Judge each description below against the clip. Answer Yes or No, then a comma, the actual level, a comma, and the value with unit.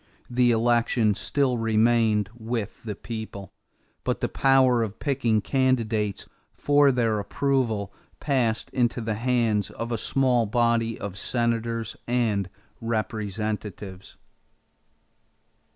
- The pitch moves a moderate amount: No, narrow, 2.2 semitones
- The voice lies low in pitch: Yes, low, 115 Hz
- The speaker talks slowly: Yes, slow, 105 wpm